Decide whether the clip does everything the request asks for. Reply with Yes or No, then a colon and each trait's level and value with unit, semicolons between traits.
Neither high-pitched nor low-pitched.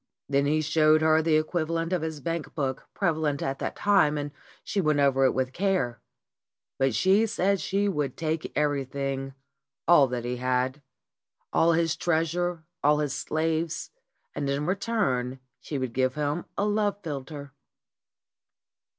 Yes: medium, 150 Hz